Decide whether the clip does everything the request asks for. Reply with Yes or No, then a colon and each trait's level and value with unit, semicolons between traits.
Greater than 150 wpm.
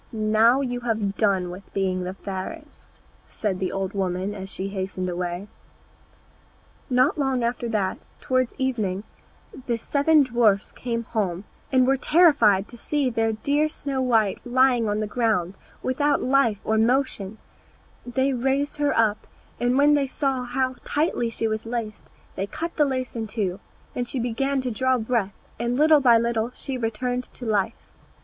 Yes: average, 165 wpm